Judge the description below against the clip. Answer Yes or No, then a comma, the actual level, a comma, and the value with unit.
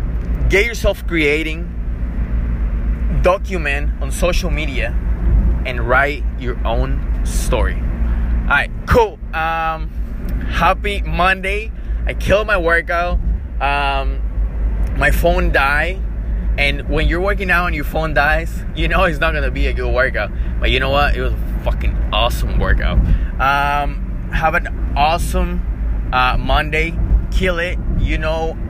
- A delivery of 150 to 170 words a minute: No, slow, 135 wpm